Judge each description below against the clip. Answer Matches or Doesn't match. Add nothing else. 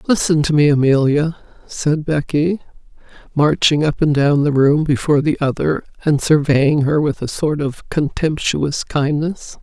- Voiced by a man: Doesn't match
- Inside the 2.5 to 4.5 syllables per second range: Matches